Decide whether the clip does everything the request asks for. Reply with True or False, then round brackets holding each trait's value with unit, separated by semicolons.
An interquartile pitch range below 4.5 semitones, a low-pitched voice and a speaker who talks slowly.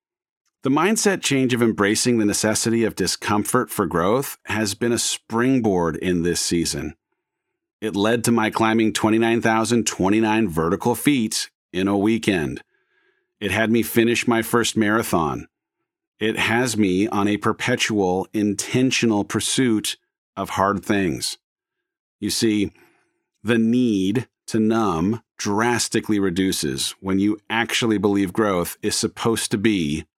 True (2.6 semitones; 110 Hz; 125 wpm)